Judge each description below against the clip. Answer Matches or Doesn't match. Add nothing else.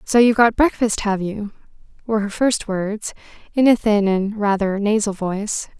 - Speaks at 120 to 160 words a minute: Doesn't match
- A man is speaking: Doesn't match